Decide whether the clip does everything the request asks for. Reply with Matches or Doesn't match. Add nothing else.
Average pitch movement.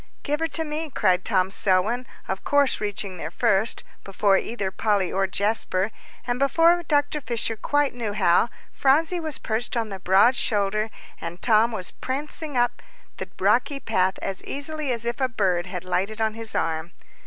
Doesn't match